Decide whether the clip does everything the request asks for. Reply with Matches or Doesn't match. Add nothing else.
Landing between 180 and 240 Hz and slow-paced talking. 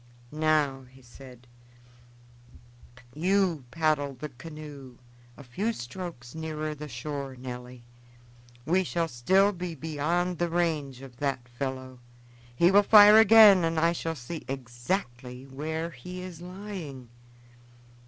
Doesn't match